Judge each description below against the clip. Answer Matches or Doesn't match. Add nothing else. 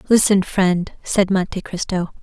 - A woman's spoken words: Matches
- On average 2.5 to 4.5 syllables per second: Matches